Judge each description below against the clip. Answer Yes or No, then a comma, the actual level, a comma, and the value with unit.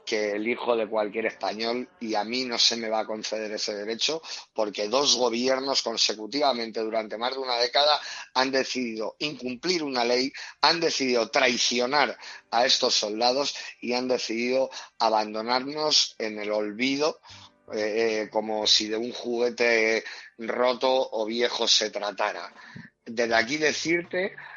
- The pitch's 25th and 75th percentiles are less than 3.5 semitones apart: Yes, average, 3.1 semitones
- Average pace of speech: Yes, average, 140 wpm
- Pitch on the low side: Yes, low, 120 Hz